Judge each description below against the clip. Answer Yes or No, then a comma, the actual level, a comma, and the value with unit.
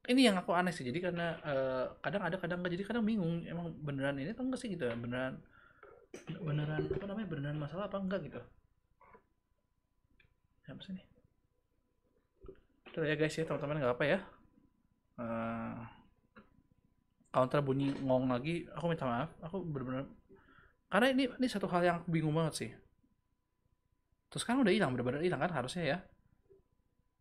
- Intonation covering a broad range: Yes, wide, 6.4 semitones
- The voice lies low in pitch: No, medium, 155 Hz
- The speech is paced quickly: Yes, fast, 160 wpm